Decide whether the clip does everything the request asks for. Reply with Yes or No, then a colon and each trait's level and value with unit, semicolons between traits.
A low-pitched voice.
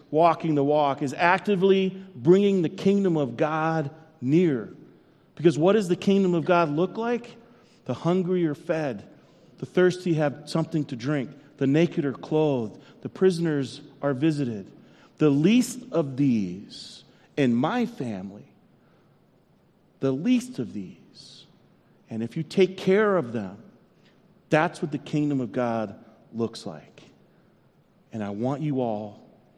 No: medium, 155 Hz